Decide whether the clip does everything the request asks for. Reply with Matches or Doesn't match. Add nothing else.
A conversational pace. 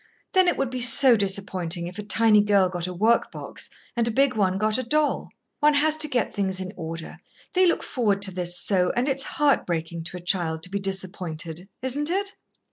Doesn't match